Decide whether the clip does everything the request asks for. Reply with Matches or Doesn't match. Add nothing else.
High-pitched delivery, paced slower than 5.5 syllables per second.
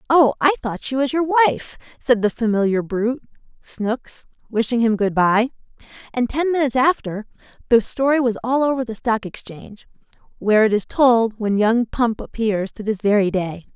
Matches